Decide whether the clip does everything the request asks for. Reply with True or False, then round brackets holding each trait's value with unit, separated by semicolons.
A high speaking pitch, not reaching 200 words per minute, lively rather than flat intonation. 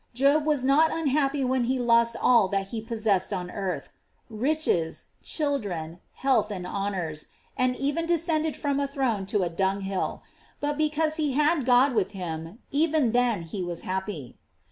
True (240 Hz; 165 wpm; 7.0 semitones)